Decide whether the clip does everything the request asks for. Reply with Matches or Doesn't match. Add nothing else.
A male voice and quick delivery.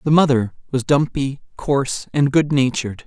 Doesn't match